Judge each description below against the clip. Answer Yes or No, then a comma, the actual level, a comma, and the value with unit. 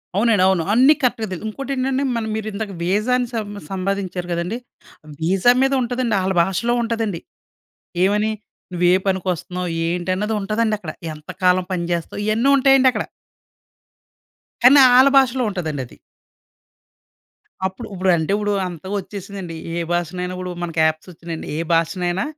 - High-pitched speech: Yes, high, 195 Hz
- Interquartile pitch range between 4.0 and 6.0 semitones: Yes, average, 4.4 semitones